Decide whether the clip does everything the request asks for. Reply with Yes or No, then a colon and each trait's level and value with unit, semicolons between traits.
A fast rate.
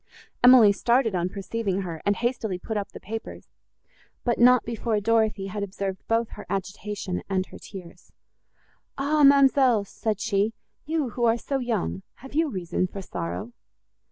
No: average, 155 wpm